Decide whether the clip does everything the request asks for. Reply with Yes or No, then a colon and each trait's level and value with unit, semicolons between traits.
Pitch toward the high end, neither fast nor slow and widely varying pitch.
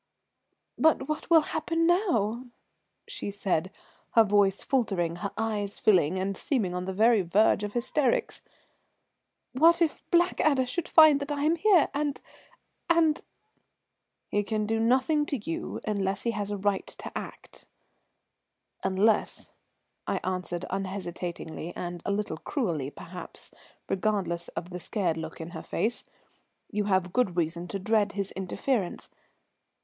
Yes: high, 205 Hz; average, 145 wpm; wide, 6.6 semitones